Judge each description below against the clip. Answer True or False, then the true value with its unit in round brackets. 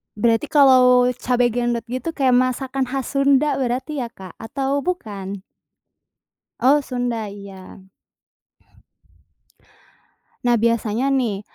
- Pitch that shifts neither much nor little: True (3.1 semitones)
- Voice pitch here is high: True (250 Hz)